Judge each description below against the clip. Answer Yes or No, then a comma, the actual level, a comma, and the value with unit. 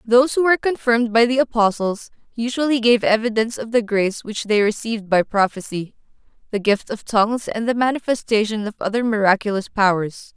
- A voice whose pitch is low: No, high, 220 Hz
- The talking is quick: No, average, 170 wpm